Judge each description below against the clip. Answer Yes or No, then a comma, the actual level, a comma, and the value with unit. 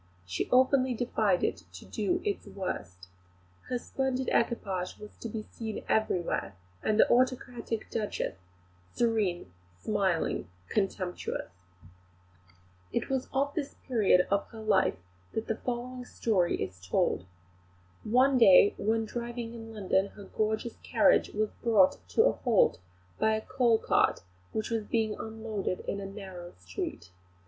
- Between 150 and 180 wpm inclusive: No, average, 140 wpm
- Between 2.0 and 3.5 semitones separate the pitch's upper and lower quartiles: No, average, 3.9 semitones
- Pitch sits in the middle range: No, high, 220 Hz